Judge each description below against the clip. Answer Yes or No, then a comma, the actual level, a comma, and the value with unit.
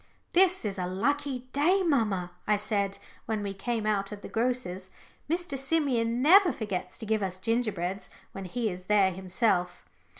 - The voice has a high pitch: Yes, high, 215 Hz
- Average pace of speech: Yes, average, 165 wpm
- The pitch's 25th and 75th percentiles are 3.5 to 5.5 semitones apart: Yes, average, 5.0 semitones